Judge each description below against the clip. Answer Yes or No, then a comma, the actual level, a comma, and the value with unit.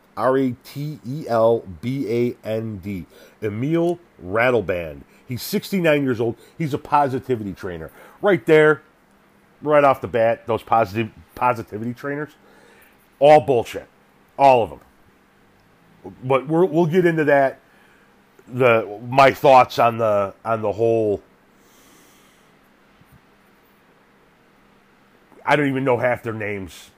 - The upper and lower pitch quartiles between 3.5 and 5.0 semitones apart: Yes, average, 4.6 semitones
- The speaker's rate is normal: No, slow, 125 wpm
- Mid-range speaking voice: No, low, 125 Hz